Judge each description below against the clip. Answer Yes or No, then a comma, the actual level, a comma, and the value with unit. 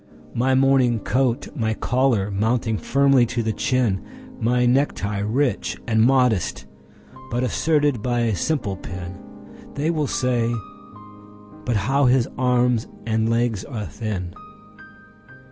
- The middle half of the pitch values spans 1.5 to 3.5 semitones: Yes, average, 3.1 semitones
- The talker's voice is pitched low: Yes, low, 120 Hz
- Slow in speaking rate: Yes, slow, 115 wpm